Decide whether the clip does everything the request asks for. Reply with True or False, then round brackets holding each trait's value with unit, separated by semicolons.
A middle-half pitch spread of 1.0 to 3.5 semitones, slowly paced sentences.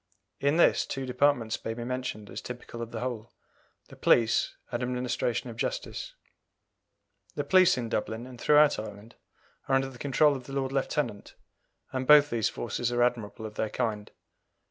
False (3.0 semitones; 175 wpm)